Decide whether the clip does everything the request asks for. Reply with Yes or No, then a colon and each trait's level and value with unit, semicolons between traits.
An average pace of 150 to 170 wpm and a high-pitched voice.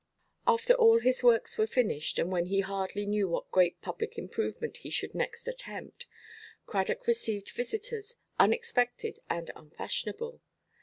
No: average, 140 wpm; very high, 405 Hz